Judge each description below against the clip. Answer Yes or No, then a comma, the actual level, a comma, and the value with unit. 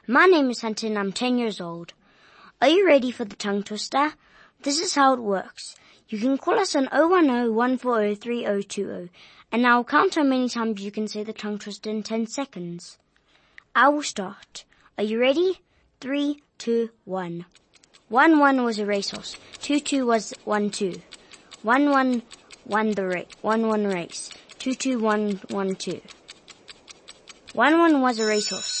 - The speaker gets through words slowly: No, average, 165 wpm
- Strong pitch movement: No, average, 4.8 semitones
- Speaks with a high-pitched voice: Yes, high, 230 Hz